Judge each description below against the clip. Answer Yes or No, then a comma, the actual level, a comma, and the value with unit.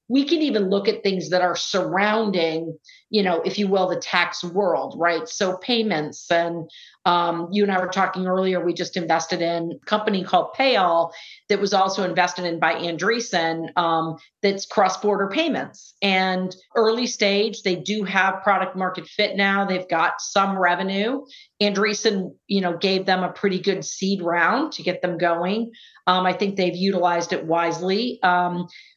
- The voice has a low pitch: No, medium, 185 Hz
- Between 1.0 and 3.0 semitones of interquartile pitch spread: Yes, narrow, 2.6 semitones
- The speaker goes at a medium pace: Yes, average, 170 wpm